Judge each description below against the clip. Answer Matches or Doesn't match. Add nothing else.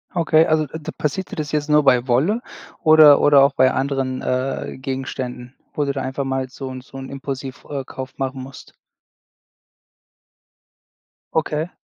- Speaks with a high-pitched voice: Doesn't match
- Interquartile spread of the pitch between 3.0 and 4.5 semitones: Doesn't match